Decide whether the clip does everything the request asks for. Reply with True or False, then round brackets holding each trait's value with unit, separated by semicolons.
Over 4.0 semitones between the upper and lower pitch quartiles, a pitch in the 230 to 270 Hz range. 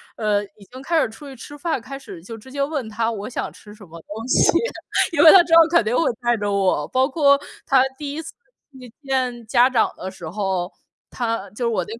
True (4.9 semitones; 240 Hz)